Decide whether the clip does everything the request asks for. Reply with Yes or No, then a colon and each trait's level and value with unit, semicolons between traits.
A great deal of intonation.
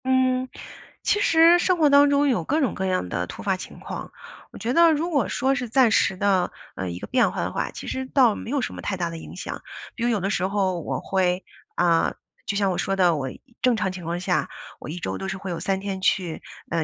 Yes: wide, 6.4 semitones